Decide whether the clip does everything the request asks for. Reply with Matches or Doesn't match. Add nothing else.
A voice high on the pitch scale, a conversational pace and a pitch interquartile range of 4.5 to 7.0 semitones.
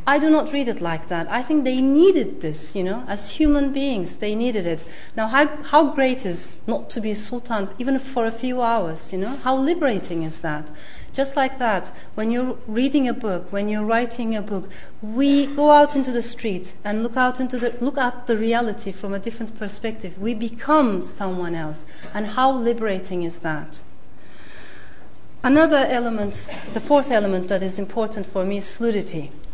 Matches